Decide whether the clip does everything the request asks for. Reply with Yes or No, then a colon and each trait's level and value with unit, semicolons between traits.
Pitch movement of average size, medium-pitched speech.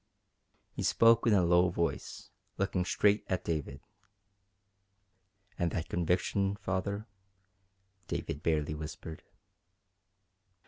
No: average, 3.4 semitones; very low, 90 Hz